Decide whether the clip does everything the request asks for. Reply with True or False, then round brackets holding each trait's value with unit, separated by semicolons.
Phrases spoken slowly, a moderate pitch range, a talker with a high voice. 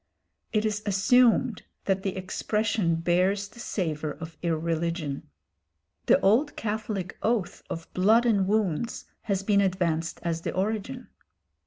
True (130 wpm; 4.3 semitones; 195 Hz)